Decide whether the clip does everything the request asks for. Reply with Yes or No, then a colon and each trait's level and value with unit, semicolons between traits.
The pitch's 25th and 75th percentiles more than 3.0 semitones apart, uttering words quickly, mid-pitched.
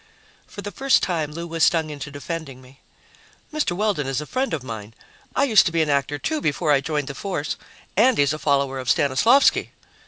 Yes: average, 5.3 semitones; fast, 210 wpm; medium, 150 Hz